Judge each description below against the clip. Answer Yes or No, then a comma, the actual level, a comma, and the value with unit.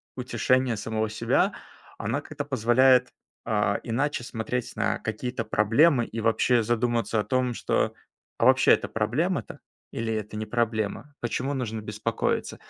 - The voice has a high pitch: No, low, 120 Hz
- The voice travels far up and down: No, narrow, 2.6 semitones